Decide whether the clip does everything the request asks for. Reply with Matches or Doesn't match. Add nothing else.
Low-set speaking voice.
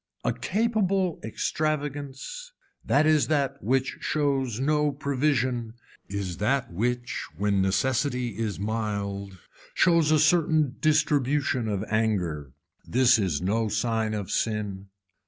Matches